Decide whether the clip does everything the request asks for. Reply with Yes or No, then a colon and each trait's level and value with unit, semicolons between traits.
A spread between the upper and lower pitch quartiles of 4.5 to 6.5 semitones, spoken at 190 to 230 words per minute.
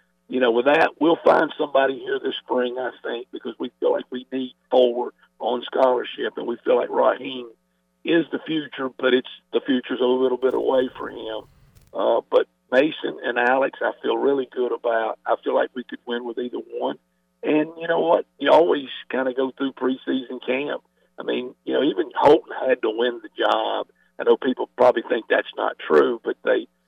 Yes: average, 5.3 semitones; fast, 205 wpm